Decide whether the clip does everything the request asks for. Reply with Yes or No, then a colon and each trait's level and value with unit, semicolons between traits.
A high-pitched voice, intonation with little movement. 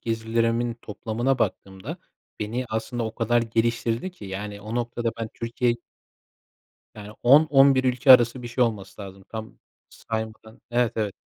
No: low, 115 Hz; narrow, 1.7 semitones